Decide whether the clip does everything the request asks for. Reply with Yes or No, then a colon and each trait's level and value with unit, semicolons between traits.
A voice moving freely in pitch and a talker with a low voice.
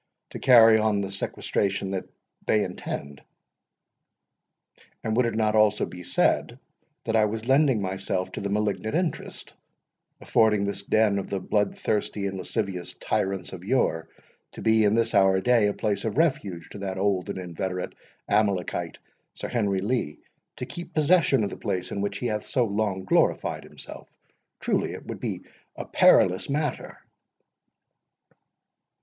No: average, 2.7 semitones; low, 105 Hz